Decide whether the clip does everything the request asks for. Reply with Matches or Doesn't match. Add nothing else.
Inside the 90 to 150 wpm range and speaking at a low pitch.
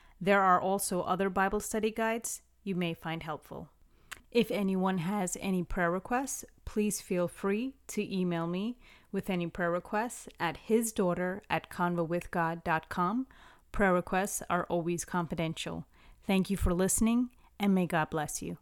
Doesn't match